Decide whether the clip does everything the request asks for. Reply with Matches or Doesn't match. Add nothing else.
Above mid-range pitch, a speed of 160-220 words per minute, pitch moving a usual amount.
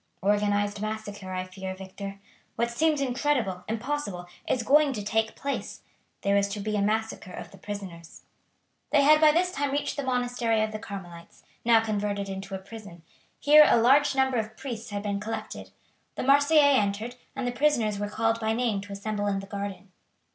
Matches